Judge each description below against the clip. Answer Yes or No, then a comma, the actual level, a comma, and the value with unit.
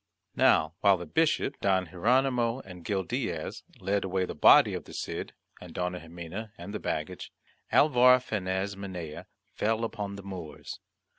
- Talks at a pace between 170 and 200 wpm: No, average, 155 wpm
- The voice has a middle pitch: No, very low, 95 Hz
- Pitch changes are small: No, average, 3.8 semitones